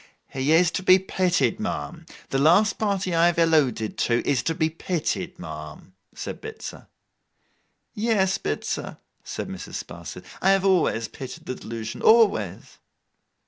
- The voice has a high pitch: No, medium, 170 Hz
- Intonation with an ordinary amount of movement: No, wide, 6.0 semitones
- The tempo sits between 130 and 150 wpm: Yes, average, 145 wpm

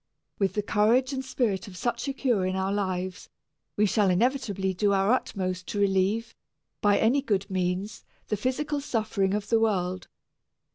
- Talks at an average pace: Yes, average, 165 wpm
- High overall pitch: Yes, high, 205 Hz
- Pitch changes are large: No, average, 3.7 semitones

